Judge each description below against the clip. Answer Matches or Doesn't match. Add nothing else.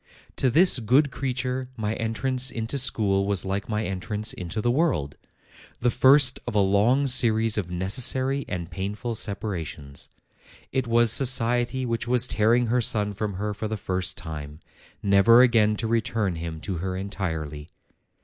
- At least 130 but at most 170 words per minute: Matches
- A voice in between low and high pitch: Doesn't match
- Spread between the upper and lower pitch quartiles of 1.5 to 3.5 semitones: Doesn't match